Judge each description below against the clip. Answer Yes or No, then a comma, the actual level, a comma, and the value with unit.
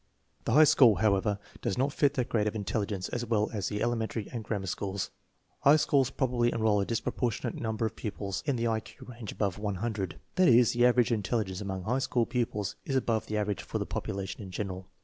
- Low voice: Yes, low, 110 Hz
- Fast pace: Yes, fast, 220 wpm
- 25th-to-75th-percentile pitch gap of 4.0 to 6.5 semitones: No, average, 3.0 semitones